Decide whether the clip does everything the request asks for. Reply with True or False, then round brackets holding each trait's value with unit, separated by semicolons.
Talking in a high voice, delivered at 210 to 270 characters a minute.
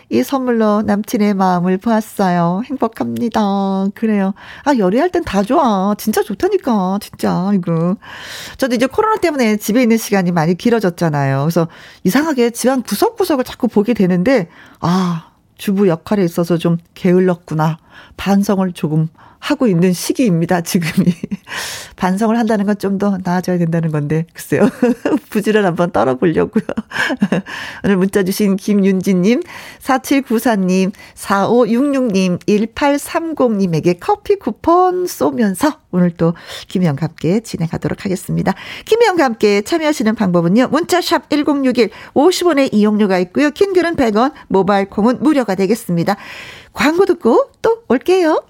False (210 Hz; 300 characters per minute)